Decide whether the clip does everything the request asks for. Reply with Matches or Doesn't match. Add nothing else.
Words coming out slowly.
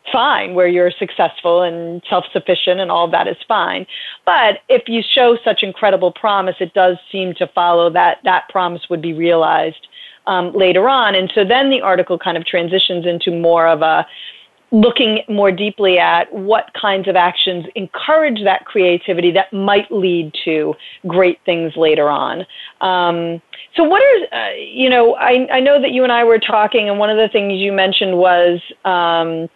Doesn't match